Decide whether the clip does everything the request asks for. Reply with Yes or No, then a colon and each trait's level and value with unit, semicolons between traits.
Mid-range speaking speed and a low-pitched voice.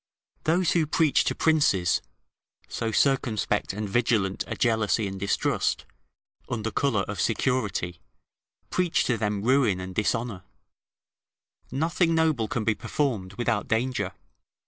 No: slow, 125 wpm; low, 115 Hz